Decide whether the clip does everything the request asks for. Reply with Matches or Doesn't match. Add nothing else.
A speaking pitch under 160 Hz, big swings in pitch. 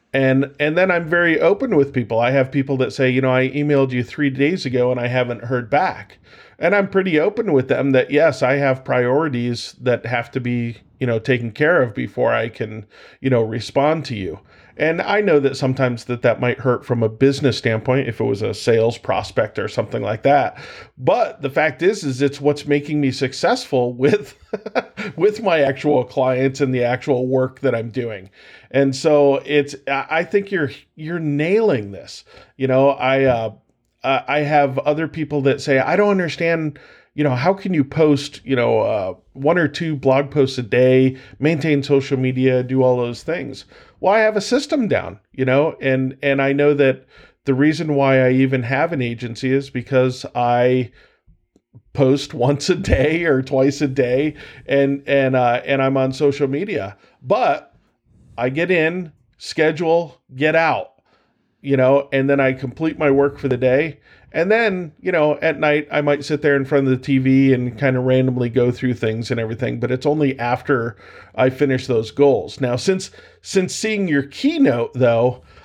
Doesn't match